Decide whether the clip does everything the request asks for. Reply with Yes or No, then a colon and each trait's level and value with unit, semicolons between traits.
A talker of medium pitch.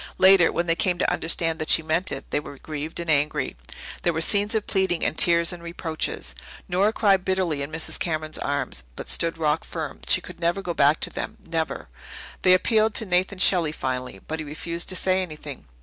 Yes: medium, 165 Hz